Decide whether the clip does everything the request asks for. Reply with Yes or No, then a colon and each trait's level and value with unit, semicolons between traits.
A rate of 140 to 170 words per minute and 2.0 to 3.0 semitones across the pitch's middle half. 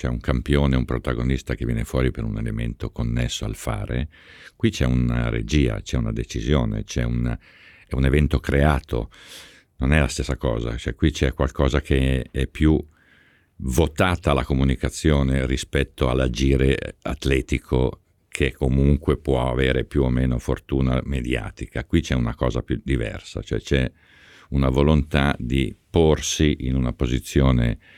Yes: average, 150 wpm; narrow, 2.5 semitones